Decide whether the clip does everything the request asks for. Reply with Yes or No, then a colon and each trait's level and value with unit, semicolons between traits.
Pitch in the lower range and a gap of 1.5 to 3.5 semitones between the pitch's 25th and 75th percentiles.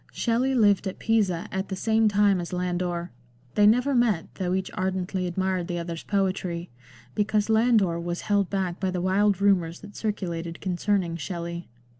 No: high, 190 Hz; average, 2.9 semitones